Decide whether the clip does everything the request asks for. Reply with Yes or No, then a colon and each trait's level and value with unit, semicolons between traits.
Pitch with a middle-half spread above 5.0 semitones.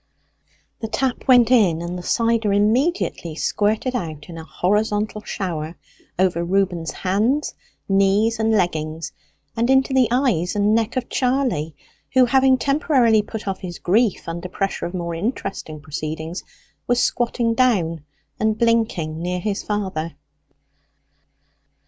Yes: wide, 5.4 semitones